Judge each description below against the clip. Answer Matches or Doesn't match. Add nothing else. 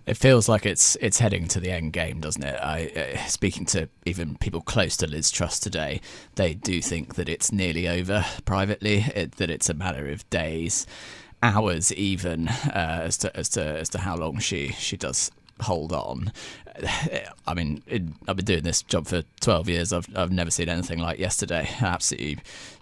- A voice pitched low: Matches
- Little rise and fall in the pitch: Doesn't match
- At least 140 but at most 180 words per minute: Doesn't match